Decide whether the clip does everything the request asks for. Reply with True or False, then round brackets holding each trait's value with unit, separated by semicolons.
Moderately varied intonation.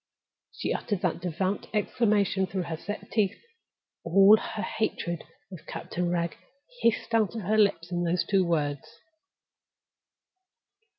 True (3.4 semitones)